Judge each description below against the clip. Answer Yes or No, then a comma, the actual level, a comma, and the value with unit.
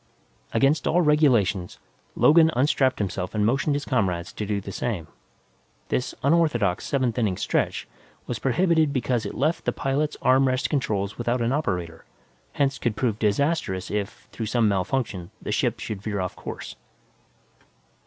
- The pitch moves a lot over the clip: Yes, wide, 5.8 semitones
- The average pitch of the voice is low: Yes, low, 120 Hz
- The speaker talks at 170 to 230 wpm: No, average, 155 wpm